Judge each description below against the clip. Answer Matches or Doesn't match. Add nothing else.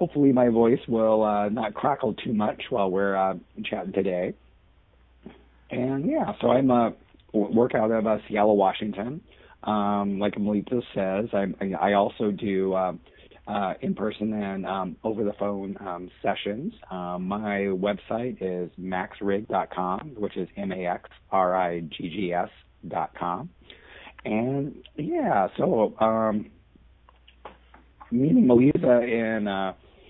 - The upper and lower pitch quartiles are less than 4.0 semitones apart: Matches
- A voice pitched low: Matches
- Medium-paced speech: Doesn't match